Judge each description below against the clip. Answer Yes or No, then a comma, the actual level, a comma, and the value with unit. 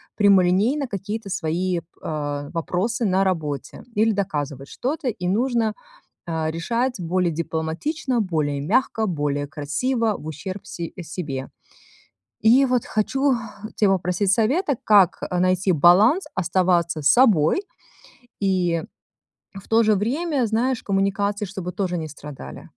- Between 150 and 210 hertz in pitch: Yes, high, 190 Hz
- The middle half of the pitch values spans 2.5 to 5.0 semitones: No, wide, 5.4 semitones